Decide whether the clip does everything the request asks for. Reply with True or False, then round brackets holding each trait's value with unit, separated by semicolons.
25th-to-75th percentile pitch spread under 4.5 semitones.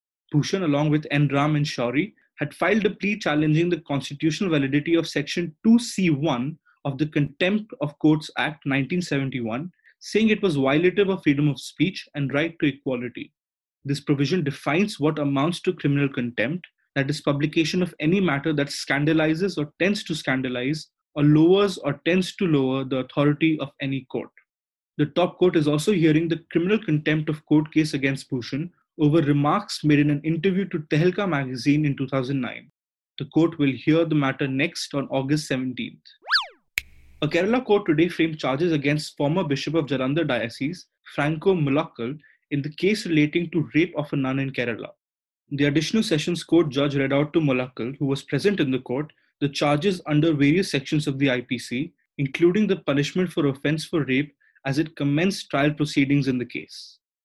True (3.1 semitones)